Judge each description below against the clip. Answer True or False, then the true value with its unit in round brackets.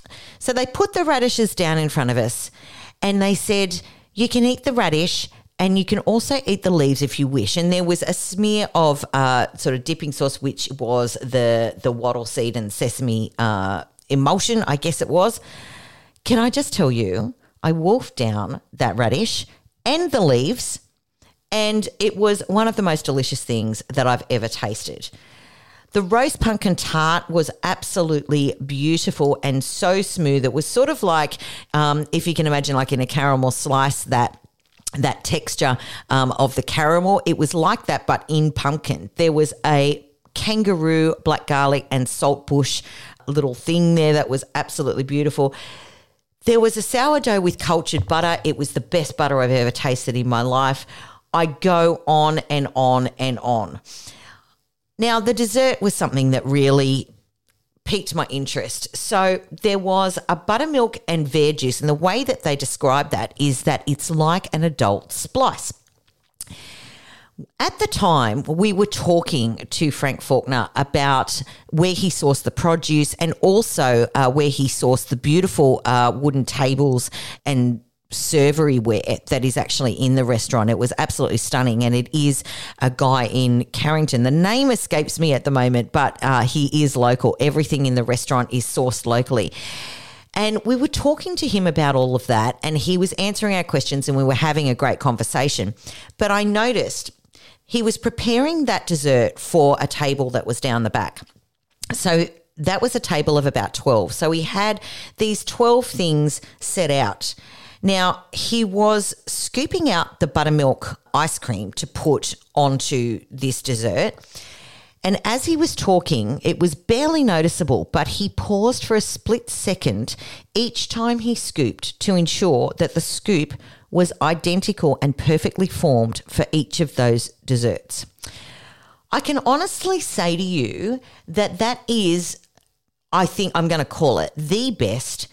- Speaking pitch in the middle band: True (150 Hz)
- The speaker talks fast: False (165 wpm)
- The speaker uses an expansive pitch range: True (6.4 semitones)